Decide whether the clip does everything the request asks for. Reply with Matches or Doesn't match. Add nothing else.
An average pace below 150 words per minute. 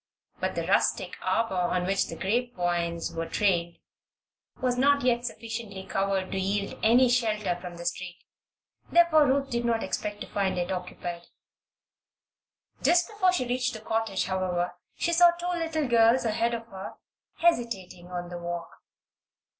Doesn't match